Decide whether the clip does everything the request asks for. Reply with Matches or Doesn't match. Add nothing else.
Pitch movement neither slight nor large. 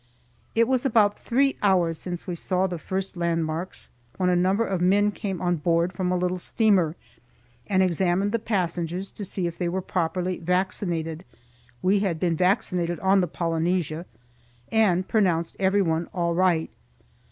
Doesn't match